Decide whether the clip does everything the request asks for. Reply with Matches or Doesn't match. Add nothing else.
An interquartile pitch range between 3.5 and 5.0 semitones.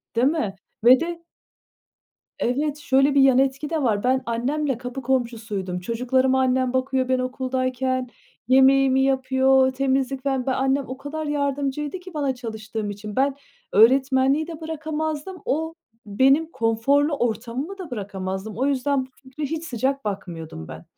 Doesn't match